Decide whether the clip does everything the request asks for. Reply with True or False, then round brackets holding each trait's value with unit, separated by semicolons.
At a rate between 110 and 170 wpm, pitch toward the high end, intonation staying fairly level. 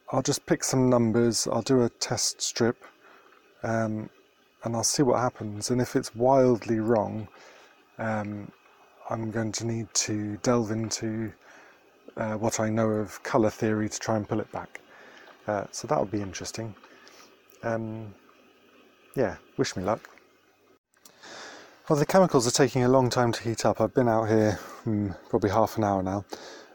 False (165 wpm; 115 Hz; 2.2 semitones)